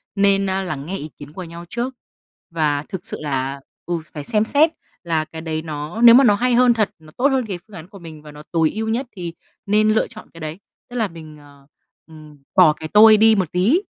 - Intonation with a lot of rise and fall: Yes, wide, 5.8 semitones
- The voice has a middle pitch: Yes, medium, 175 Hz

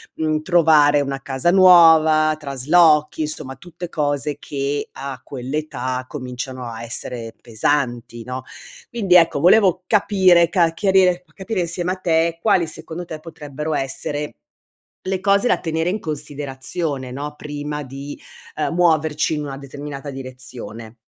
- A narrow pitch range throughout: No, average, 4.0 semitones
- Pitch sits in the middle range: Yes, medium, 150 Hz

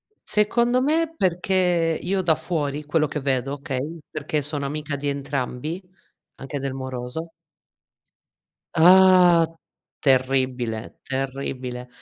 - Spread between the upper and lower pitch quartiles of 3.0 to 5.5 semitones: Yes, average, 4.6 semitones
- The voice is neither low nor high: Yes, medium, 145 Hz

